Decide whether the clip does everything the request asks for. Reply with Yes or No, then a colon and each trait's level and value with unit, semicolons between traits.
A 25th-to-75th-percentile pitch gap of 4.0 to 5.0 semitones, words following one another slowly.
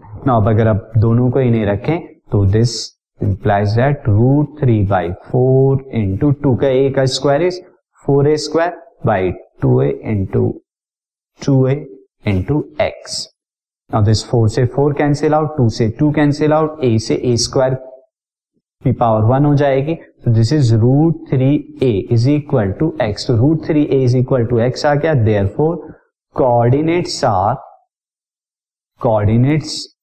No: average, 4.7 semitones; average, 135 wpm